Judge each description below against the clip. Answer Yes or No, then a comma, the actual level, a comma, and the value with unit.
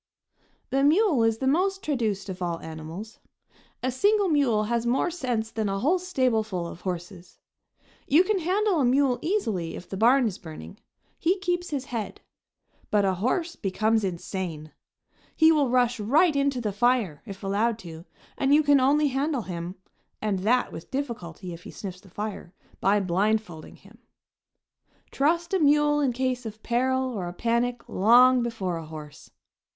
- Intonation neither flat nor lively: No, wide, 6.6 semitones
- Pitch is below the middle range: No, high, 235 Hz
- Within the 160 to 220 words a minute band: Yes, average, 165 wpm